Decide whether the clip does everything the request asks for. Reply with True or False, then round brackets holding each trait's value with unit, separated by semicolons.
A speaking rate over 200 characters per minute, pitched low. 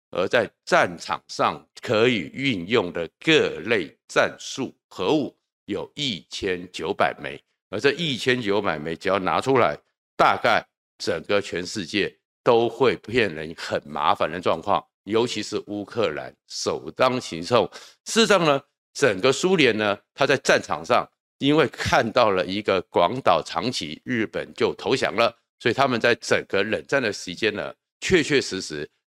True (225 characters per minute; 130 Hz)